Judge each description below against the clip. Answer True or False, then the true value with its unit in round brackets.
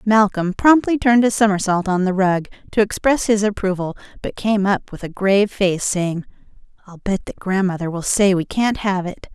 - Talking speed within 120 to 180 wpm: False (195 wpm)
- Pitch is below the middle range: False (195 Hz)